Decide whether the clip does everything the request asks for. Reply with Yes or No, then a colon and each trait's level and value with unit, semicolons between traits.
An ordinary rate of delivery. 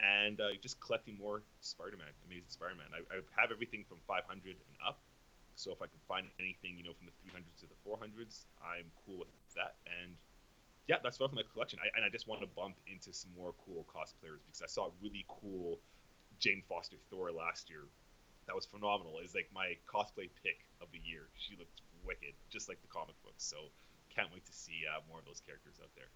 No: fast, 220 wpm